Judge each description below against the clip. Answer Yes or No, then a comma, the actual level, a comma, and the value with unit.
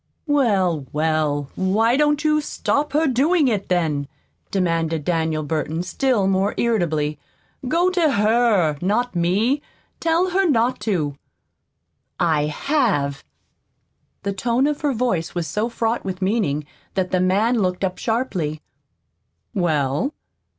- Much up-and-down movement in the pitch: Yes, wide, 7.6 semitones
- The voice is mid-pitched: No, high, 195 Hz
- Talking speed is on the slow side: Yes, slow, 130 wpm